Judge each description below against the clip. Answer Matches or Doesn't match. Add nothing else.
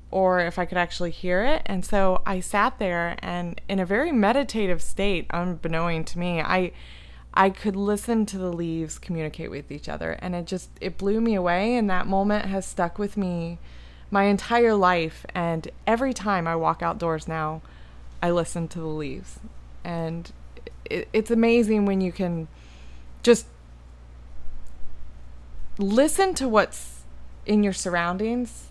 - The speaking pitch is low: Doesn't match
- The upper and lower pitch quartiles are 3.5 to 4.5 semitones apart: Matches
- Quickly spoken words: Doesn't match